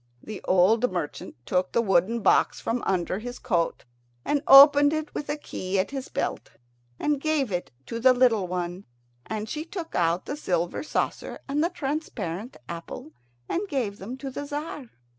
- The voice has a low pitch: No, high, 235 Hz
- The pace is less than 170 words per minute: No, average, 175 wpm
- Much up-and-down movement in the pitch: Yes, wide, 7.6 semitones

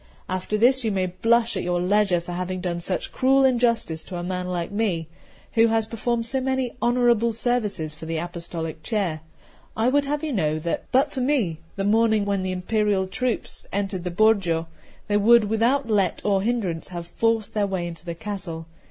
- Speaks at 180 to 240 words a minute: Yes, average, 195 wpm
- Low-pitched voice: No, high, 205 Hz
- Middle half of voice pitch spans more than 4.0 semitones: Yes, average, 4.7 semitones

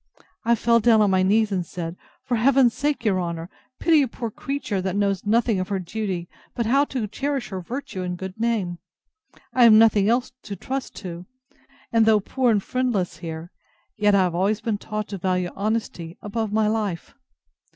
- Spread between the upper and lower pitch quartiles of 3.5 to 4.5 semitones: Yes, average, 3.9 semitones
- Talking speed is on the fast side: No, average, 195 wpm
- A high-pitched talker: Yes, high, 210 Hz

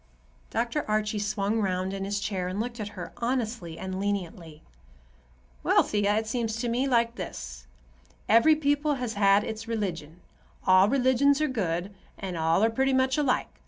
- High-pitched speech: Yes, high, 215 Hz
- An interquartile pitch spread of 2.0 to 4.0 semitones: No, average, 4.5 semitones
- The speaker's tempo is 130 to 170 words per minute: Yes, average, 165 wpm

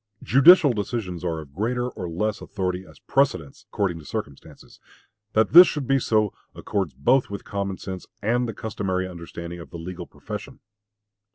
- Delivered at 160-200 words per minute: Yes, average, 165 wpm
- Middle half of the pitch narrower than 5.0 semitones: No, wide, 5.4 semitones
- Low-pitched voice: Yes, low, 100 Hz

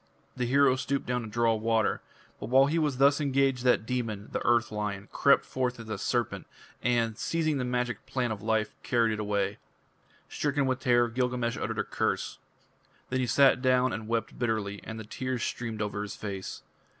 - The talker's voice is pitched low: Yes, low, 120 Hz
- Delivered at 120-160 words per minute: No, average, 190 wpm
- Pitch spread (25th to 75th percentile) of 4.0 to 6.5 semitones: No, average, 2.8 semitones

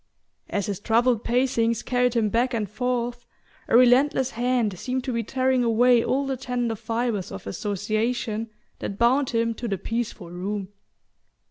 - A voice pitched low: No, high, 235 Hz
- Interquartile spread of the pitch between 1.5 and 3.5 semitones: Yes, narrow, 2.5 semitones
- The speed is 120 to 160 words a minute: Yes, average, 155 wpm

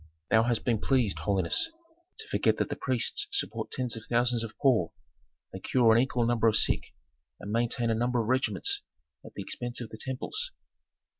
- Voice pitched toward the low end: Yes, low, 120 Hz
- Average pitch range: No, narrow, 2.3 semitones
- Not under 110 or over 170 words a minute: No, average, 190 wpm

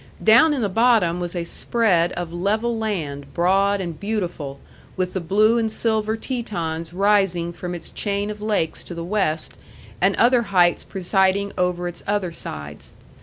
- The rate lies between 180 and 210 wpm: No, average, 165 wpm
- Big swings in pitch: No, average, 3.8 semitones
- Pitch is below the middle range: No, high, 190 Hz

